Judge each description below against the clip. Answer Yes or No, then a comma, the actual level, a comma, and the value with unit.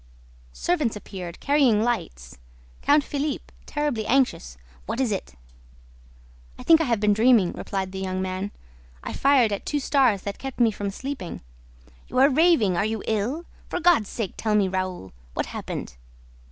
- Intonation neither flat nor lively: No, wide, 6.2 semitones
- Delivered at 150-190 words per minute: Yes, average, 160 wpm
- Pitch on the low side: No, high, 220 Hz